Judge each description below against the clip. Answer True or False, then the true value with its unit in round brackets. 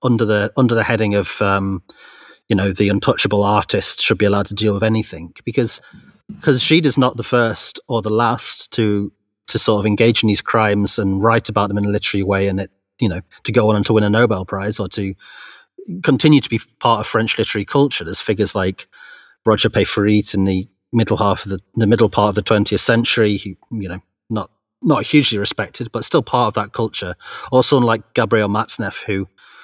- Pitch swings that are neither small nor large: False (2.3 semitones)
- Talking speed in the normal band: False (210 wpm)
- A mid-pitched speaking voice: False (105 Hz)